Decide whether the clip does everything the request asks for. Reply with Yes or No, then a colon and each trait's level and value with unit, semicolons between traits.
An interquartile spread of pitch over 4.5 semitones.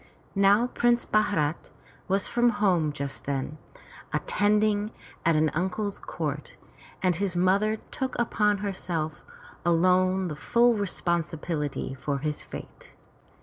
Yes: average, 5.1 semitones